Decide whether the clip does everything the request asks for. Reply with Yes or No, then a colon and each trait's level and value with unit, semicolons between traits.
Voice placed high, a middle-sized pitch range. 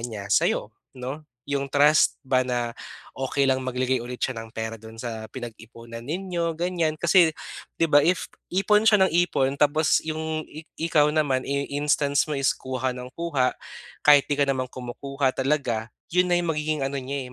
No: medium, 140 Hz; average, 3.6 semitones